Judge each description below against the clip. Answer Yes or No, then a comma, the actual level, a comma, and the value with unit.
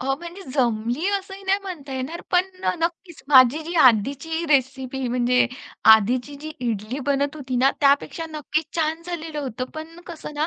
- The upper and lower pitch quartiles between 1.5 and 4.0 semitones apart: No, average, 4.4 semitones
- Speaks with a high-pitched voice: Yes, very high, 290 Hz